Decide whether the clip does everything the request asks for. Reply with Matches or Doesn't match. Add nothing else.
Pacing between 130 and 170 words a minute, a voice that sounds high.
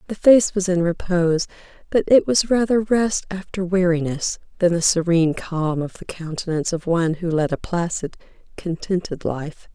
Doesn't match